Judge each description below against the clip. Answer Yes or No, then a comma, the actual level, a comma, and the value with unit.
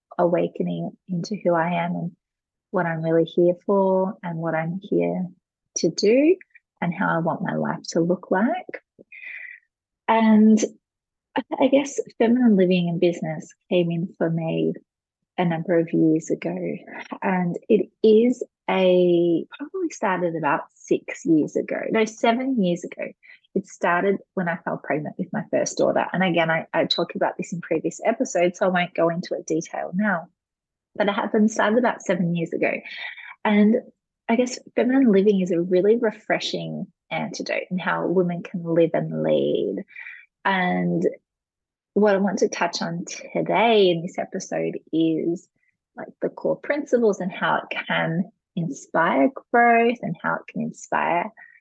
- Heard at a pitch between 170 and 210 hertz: Yes, medium, 185 Hz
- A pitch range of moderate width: Yes, average, 4.7 semitones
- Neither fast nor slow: Yes, average, 160 wpm